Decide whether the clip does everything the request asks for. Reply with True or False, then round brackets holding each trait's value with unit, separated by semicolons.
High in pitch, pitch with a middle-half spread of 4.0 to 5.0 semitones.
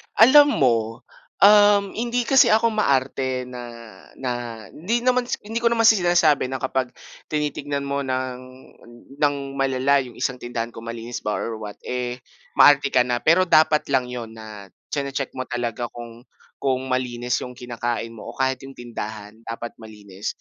False (130 Hz; 4.4 semitones)